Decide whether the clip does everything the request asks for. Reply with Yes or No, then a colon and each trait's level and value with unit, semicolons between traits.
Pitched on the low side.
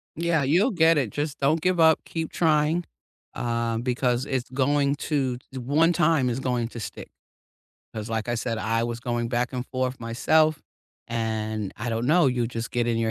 Yes: low, 125 Hz